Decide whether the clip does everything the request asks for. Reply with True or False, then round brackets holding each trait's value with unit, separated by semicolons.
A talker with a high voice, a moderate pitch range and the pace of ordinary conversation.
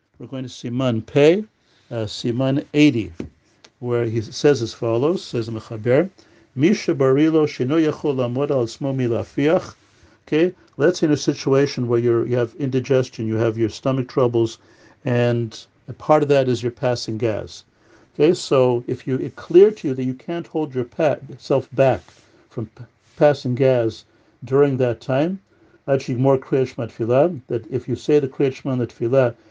False (125 Hz; 3.4 semitones; 155 wpm)